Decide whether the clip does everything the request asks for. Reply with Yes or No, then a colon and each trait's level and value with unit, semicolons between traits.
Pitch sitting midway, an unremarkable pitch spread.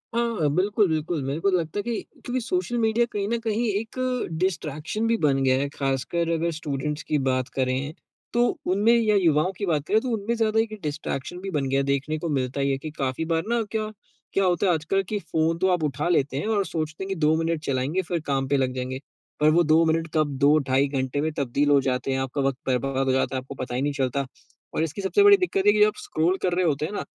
No: medium, 160 Hz; wide, 6.4 semitones